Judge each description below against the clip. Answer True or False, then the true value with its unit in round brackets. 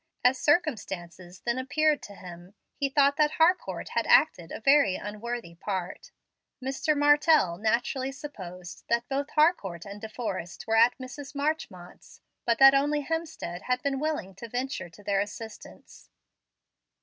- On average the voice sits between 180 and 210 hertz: False (245 Hz)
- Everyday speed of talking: True (150 wpm)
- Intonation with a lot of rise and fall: True (6.9 semitones)